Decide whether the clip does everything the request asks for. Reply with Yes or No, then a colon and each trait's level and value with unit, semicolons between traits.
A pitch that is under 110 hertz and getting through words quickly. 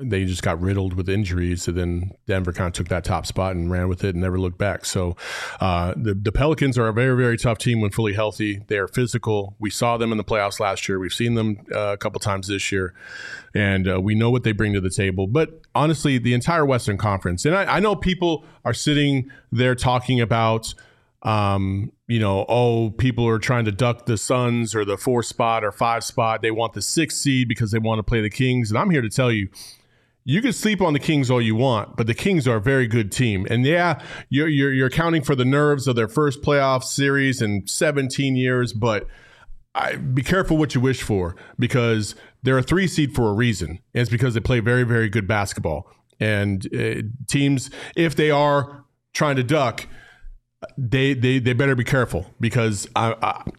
No: low, 120 Hz; fast, 220 wpm